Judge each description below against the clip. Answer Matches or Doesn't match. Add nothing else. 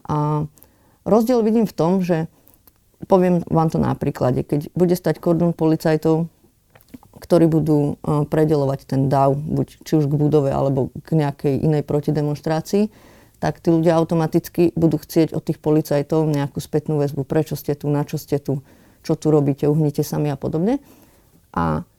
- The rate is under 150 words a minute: Doesn't match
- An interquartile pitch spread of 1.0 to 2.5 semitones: Matches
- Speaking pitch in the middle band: Matches